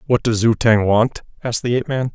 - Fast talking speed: Yes, fast, 250 wpm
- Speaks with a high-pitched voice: No, low, 115 Hz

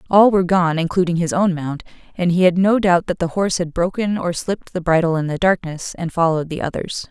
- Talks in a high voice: No, medium, 175 Hz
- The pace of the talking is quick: Yes, fast, 235 wpm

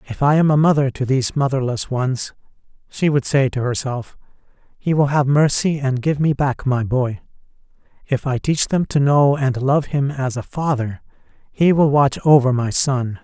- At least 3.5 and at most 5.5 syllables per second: Yes, 4.7 syllables/s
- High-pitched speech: No, low, 135 Hz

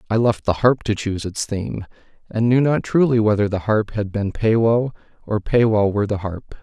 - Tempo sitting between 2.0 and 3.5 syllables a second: No, 5.3 syllables/s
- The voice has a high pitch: No, low, 110 Hz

